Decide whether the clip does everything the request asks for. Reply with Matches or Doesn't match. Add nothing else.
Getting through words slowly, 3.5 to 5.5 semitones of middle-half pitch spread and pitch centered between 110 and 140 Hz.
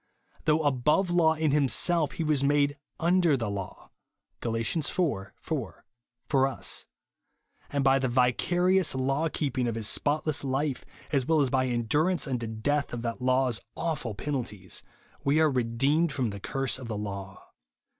Doesn't match